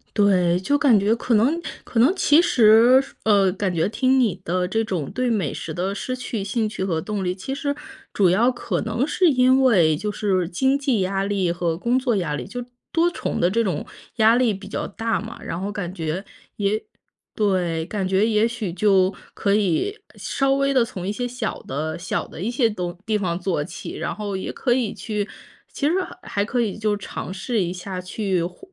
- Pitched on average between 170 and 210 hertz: Yes, high, 205 Hz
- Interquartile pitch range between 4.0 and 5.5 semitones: Yes, average, 4.6 semitones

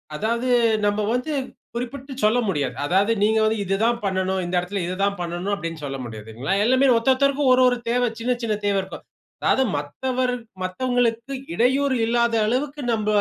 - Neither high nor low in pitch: No, high, 230 Hz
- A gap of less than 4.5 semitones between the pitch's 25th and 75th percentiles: No, average, 5.0 semitones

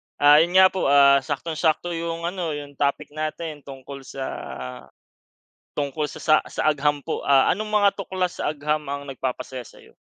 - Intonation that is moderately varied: Yes, average, 3.1 semitones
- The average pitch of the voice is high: No, medium, 150 Hz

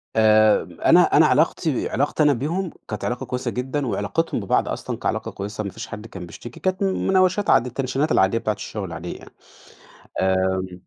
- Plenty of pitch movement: Yes, wide, 6.9 semitones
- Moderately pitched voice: No, low, 125 Hz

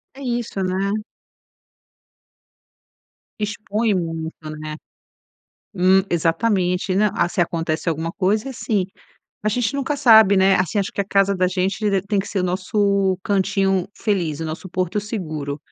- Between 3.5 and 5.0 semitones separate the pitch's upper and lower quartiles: No, average, 2.8 semitones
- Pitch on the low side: No, high, 190 Hz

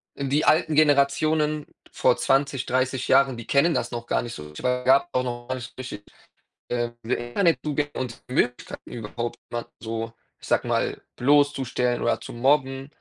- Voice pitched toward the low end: Yes, low, 130 Hz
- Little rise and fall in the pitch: No, average, 3.1 semitones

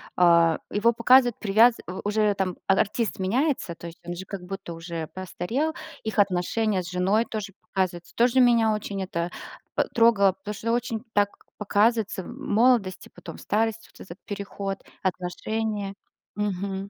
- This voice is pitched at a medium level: No, high, 200 Hz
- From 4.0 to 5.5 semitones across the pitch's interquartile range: No, average, 3.2 semitones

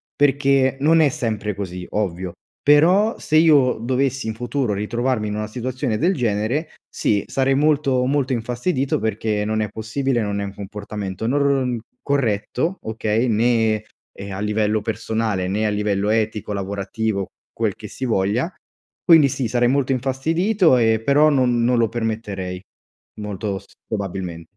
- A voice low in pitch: Yes, low, 115 Hz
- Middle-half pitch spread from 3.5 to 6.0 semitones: Yes, average, 4.4 semitones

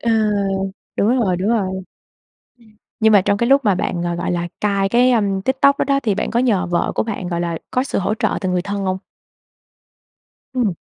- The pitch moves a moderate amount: Yes, average, 4.4 semitones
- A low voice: No, high, 200 Hz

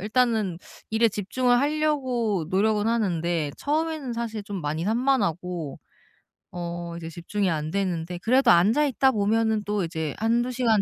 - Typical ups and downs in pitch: No, wide, 5.7 semitones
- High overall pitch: Yes, high, 210 Hz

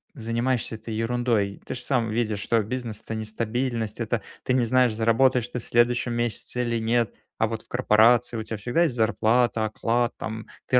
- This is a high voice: No, low, 115 Hz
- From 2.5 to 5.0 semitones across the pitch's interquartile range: No, narrow, 1.7 semitones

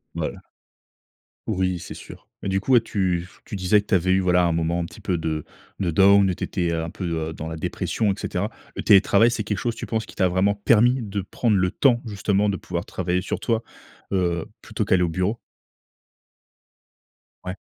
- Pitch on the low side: Yes, very low, 95 Hz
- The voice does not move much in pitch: No, average, 3.0 semitones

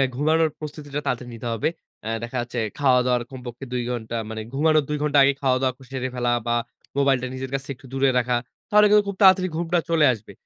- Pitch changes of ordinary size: Yes, average, 3.5 semitones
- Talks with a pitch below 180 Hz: Yes, low, 135 Hz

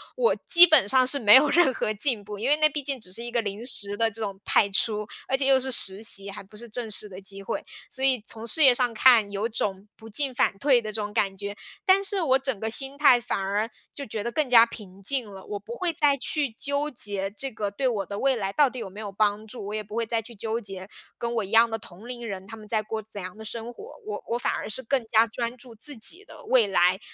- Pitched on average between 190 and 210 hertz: No, high, 225 Hz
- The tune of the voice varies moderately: Yes, average, 4.2 semitones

